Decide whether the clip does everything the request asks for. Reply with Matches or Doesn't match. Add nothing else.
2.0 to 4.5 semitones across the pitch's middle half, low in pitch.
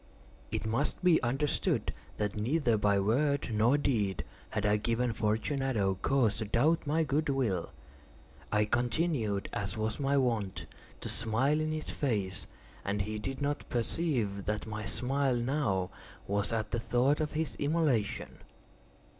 Doesn't match